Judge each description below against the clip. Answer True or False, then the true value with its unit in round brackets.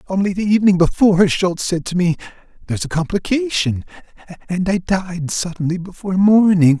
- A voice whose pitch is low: False (185 Hz)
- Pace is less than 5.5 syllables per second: False (5.6 syllables/s)